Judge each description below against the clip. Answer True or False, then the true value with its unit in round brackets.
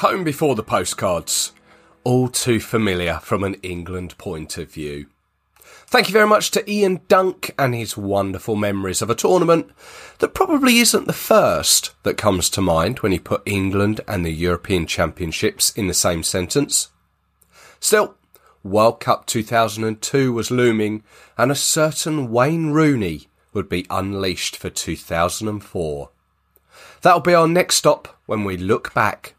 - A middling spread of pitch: False (8.7 semitones)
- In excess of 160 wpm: False (150 wpm)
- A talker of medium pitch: False (105 Hz)